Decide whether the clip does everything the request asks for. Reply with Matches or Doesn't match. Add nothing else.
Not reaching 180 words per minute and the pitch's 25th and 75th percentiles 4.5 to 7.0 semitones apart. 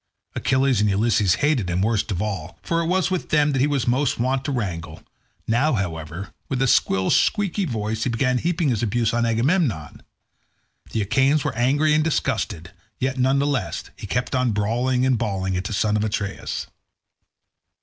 Doesn't match